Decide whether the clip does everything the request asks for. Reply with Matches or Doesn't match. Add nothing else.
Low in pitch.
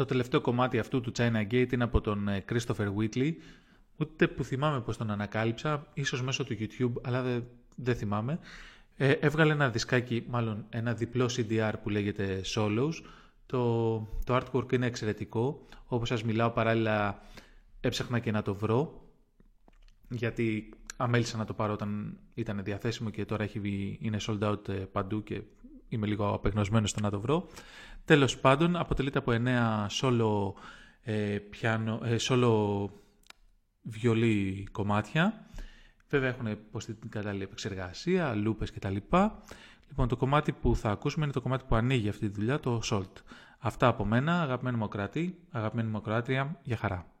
Matches